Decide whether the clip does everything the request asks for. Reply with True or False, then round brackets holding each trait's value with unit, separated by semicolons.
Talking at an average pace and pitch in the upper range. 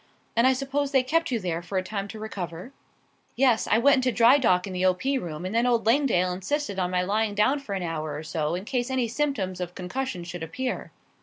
False (240 wpm; 215 Hz)